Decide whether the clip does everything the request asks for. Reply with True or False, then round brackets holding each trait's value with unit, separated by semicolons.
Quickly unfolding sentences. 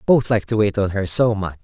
True (295 wpm)